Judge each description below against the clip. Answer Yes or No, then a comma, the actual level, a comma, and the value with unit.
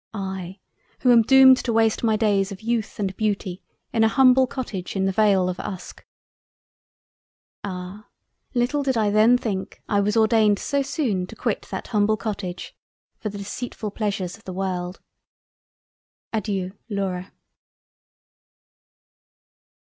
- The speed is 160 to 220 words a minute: No, average, 140 wpm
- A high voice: Yes, high, 210 Hz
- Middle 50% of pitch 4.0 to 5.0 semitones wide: No, average, 3.0 semitones